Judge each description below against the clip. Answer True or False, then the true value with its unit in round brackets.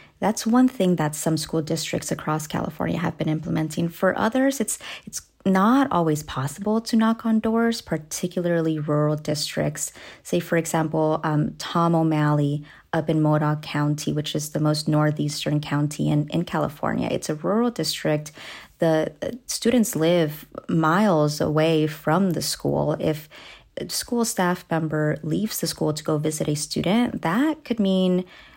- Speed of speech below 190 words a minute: True (155 wpm)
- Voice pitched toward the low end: False (160 Hz)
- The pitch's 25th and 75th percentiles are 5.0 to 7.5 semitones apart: False (4.0 semitones)